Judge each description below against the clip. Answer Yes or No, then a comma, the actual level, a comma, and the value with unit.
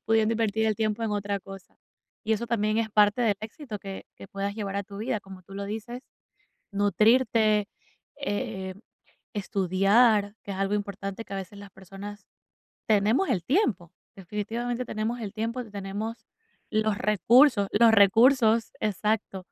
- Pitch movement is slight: Yes, narrow, 2.2 semitones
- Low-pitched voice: No, high, 210 Hz